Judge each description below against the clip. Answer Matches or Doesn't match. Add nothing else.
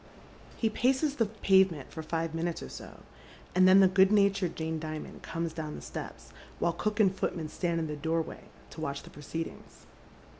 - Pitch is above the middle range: Doesn't match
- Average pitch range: Matches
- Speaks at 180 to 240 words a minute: Matches